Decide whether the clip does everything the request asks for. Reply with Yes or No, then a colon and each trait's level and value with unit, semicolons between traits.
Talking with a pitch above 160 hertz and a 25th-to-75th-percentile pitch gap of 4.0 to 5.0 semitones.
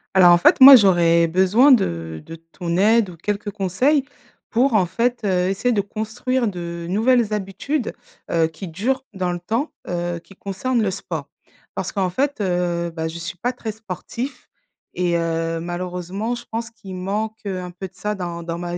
Yes: high, 190 Hz; average, 4.4 semitones